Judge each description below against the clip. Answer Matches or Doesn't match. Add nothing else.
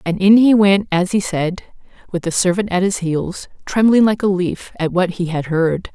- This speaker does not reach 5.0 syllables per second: Matches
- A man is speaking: Doesn't match